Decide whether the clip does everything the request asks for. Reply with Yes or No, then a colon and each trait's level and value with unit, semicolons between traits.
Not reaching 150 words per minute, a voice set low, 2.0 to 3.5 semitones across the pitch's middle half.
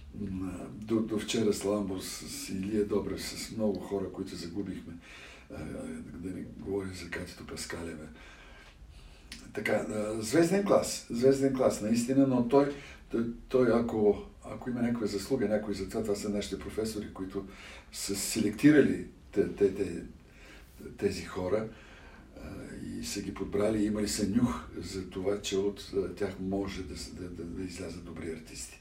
Yes: average, 135 wpm; low, 100 Hz; narrow, 2.6 semitones